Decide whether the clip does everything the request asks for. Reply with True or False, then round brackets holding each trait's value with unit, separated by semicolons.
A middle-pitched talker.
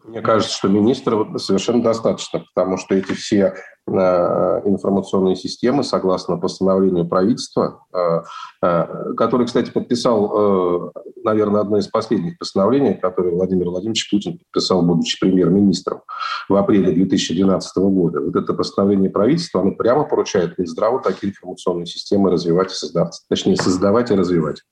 False (95 Hz)